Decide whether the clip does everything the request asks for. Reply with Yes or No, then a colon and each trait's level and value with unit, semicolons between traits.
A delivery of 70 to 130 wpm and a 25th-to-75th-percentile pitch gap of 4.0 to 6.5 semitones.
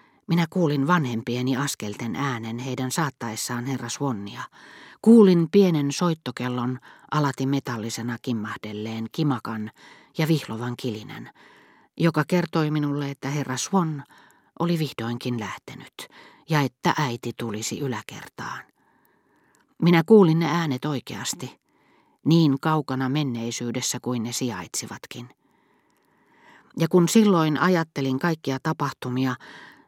Yes: average, 100 wpm; average, 5.0 semitones